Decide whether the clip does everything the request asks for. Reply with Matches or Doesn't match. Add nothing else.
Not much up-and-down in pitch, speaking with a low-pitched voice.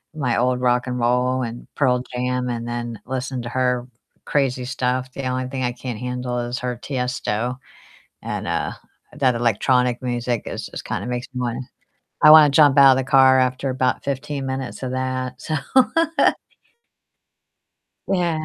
Matches